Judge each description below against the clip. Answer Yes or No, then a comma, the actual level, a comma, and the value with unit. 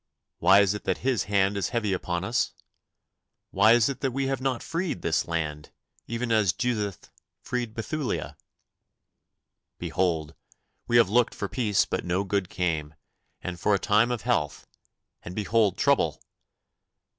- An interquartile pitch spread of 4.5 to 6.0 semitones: Yes, average, 4.8 semitones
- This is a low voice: Yes, low, 105 Hz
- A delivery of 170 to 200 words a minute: No, average, 155 wpm